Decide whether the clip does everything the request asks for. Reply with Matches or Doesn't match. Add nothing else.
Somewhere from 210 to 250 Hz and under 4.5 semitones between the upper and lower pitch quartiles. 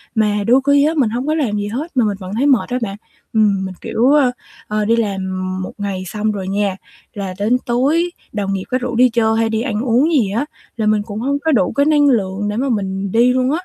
Matches